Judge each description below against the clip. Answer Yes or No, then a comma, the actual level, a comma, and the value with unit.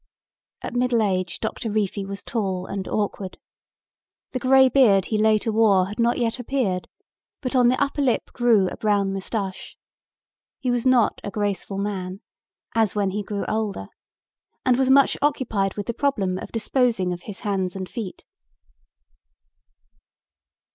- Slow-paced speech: No, average, 155 wpm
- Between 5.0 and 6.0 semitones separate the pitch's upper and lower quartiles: No, average, 4.0 semitones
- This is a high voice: Yes, high, 215 Hz